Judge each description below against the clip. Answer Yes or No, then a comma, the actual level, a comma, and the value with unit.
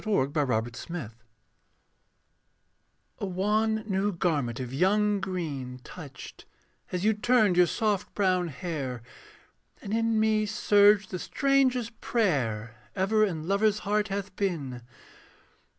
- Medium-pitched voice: No, high, 195 Hz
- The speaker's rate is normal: No, slow, 120 wpm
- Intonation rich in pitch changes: Yes, wide, 6.0 semitones